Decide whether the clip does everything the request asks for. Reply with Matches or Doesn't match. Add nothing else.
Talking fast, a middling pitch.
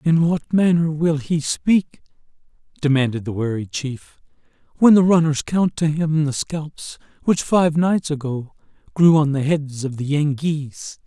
Doesn't match